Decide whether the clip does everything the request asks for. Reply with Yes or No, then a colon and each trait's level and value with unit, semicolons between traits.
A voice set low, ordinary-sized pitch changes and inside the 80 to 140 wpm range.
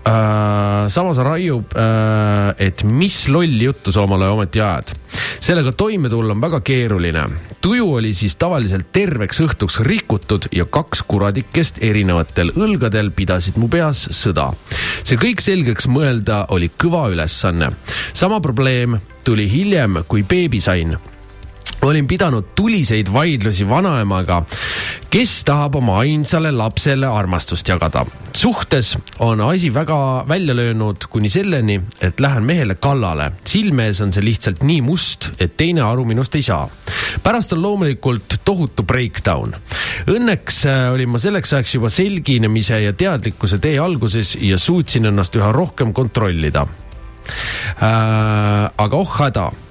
No: low, 115 Hz; wide, 6.1 semitones; slow, 135 wpm